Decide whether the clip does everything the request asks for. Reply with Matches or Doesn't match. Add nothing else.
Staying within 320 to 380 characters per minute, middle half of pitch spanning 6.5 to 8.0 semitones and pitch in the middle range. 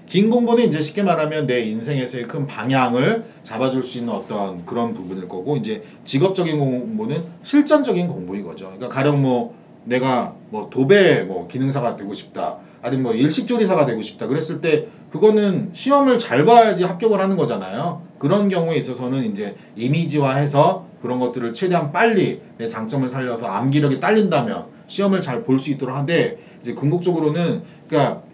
Matches